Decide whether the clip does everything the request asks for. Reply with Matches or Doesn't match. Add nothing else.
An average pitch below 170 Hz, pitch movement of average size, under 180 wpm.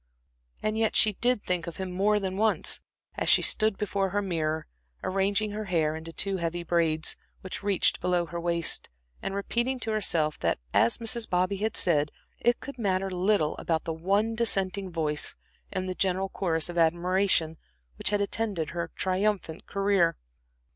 Doesn't match